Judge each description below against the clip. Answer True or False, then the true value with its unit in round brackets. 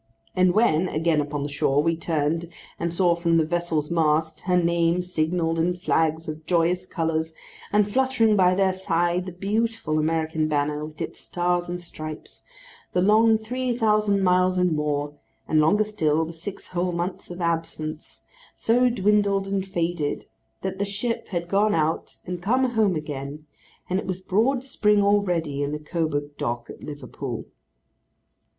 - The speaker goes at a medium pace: True (160 wpm)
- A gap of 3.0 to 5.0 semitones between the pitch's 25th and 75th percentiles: True (3.9 semitones)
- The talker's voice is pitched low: False (175 Hz)